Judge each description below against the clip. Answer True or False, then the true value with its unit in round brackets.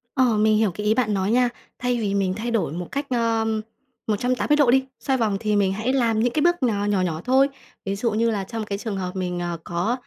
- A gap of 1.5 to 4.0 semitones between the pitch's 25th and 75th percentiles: True (3.7 semitones)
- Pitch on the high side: True (220 Hz)